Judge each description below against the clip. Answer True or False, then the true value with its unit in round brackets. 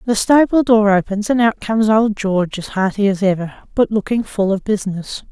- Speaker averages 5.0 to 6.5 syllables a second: True (5.5 syllables/s)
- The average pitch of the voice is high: True (210 Hz)